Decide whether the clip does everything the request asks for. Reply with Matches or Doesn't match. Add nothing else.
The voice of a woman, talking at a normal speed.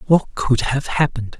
Doesn't match